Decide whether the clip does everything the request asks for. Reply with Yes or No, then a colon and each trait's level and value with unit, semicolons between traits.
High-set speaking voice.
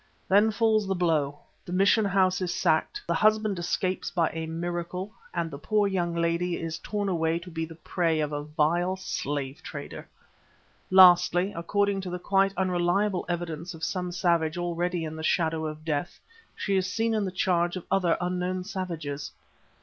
No: medium, 175 Hz